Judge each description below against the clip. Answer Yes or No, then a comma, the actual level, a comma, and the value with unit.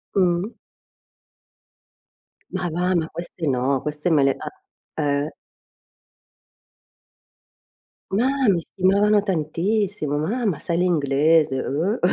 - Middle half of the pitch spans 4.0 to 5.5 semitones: Yes, average, 4.5 semitones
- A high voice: No, medium, 170 Hz